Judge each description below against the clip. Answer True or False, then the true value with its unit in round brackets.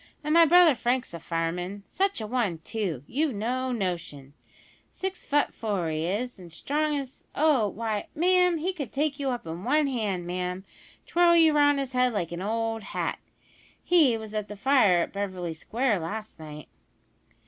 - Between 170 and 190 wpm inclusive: True (185 wpm)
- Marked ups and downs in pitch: True (8.0 semitones)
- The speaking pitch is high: True (225 Hz)